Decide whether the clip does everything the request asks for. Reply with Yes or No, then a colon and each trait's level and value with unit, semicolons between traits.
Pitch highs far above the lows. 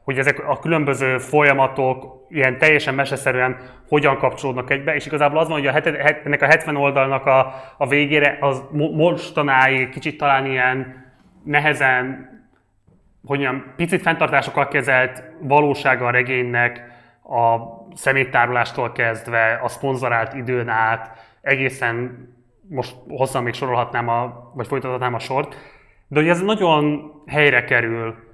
No: average, 2.8 semitones